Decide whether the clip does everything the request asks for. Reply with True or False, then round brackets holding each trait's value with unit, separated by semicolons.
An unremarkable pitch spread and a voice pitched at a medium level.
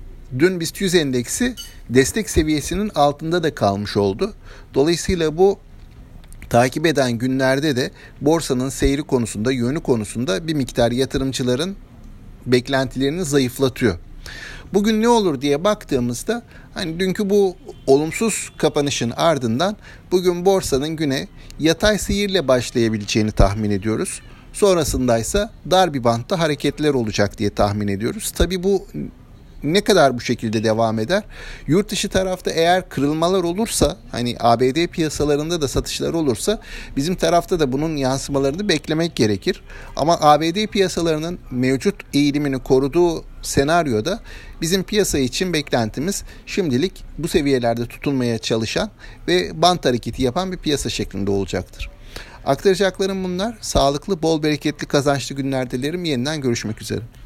False (6.6 semitones; 145 Hz)